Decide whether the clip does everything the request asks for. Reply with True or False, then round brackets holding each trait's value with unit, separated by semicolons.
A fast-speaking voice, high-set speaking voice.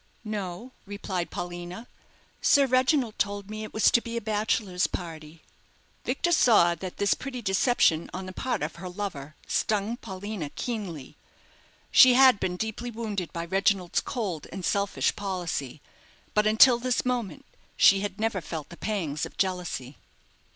False (150 wpm; 200 Hz)